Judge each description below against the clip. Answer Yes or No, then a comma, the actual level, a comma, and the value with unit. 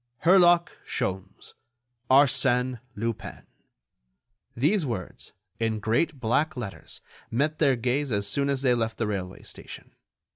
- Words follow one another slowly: Yes, slow, 115 wpm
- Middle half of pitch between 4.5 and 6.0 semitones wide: No, average, 4.1 semitones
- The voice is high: No, low, 125 Hz